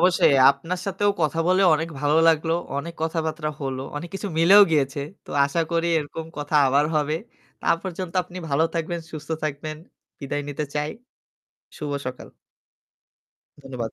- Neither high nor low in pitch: Yes, medium, 155 Hz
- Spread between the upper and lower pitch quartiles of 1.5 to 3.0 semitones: Yes, average, 2.7 semitones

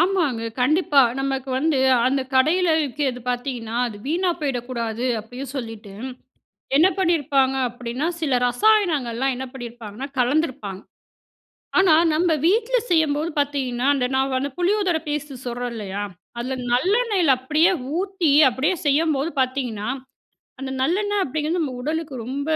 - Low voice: No, very high, 275 Hz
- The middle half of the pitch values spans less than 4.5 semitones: No, average, 4.8 semitones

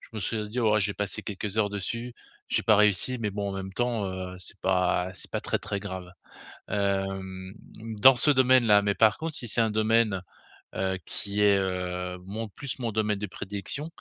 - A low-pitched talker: Yes, low, 105 Hz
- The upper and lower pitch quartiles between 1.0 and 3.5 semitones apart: Yes, average, 2.8 semitones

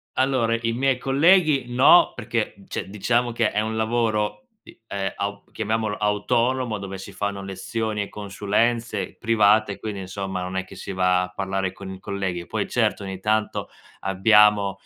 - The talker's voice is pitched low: Yes, low, 105 Hz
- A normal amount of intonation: Yes, average, 3.0 semitones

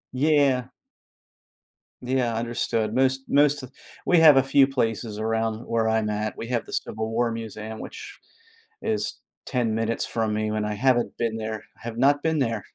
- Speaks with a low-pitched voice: Yes, low, 115 Hz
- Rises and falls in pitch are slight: No, average, 3.2 semitones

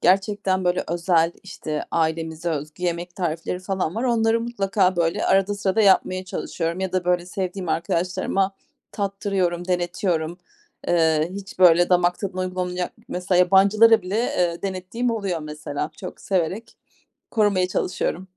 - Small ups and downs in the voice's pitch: Yes, narrow, 2.3 semitones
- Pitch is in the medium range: Yes, medium, 180 Hz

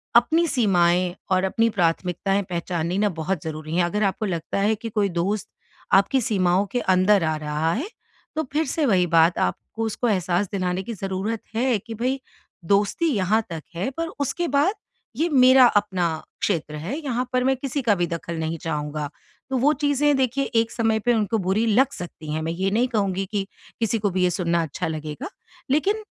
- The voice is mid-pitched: No, high, 200 Hz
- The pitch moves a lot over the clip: Yes, wide, 5.8 semitones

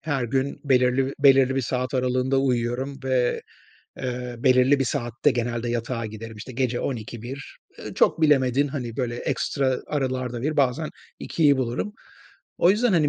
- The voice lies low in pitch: Yes, low, 130 Hz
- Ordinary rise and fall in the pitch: No, narrow, 2.2 semitones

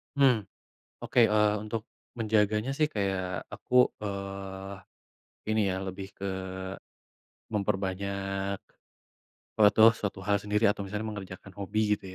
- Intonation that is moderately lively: No, narrow, 1.7 semitones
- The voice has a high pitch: No, low, 100 Hz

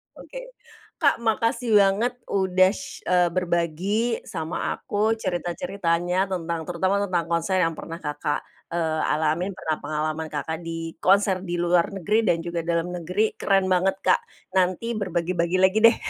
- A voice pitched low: No, medium, 180 Hz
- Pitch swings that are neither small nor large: Yes, average, 3.0 semitones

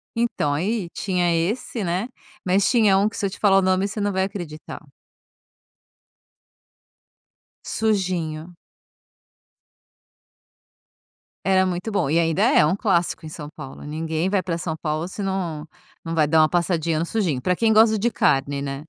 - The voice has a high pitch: No, medium, 180 Hz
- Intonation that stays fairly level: No, average, 3.9 semitones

